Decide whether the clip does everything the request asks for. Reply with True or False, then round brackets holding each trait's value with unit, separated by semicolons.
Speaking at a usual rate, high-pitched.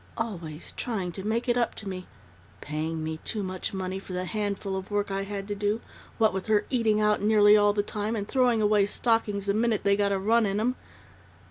False (225 wpm; 205 Hz)